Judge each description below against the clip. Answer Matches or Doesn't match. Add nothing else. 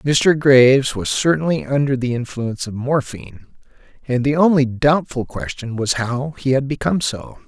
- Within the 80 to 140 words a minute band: Doesn't match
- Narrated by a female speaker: Doesn't match